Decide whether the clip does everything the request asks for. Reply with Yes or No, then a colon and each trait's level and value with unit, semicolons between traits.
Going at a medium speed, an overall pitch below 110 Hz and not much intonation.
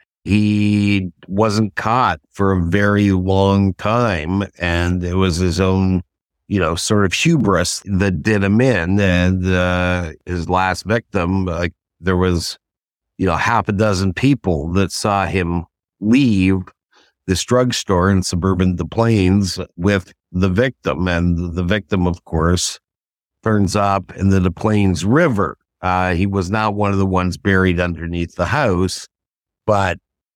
Yes: average, 150 wpm; very low, 95 Hz; narrow, 2.3 semitones